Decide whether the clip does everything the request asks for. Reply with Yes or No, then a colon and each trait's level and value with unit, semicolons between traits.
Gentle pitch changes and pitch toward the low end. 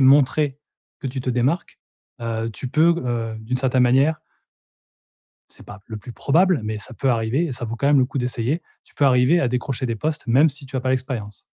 No: average, 3.3 semitones; low, 130 Hz